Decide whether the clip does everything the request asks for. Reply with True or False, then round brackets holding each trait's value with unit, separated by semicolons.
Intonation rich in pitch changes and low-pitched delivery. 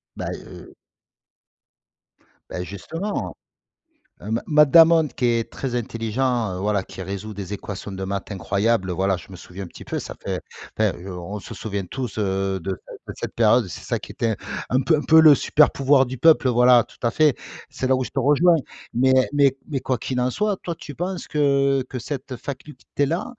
True (6.0 semitones; 125 Hz)